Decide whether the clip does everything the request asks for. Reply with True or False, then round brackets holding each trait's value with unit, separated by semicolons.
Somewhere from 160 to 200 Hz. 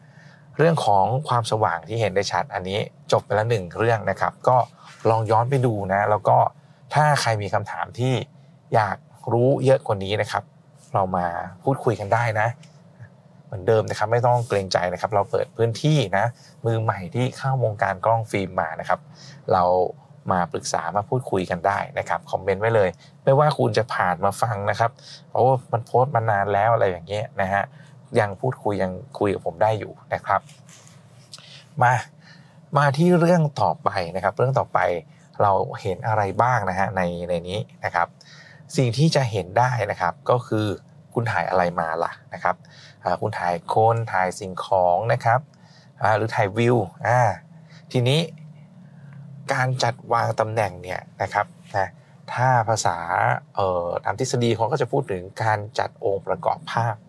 False (115 Hz)